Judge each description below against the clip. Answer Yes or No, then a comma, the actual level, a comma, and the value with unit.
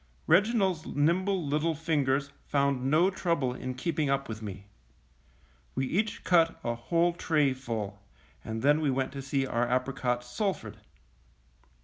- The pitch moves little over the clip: No, average, 4.6 semitones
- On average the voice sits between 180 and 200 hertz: No, medium, 140 Hz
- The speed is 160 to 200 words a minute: No, average, 140 wpm